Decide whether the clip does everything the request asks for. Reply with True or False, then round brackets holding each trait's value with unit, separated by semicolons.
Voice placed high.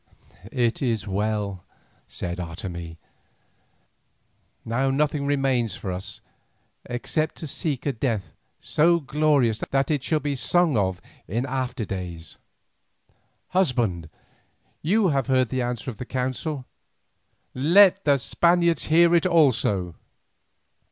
False (130 Hz)